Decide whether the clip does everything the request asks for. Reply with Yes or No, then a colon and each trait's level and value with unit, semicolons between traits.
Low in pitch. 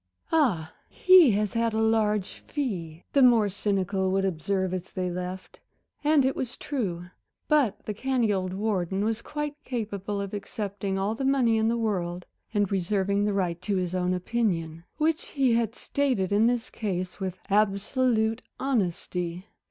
No: high, 205 Hz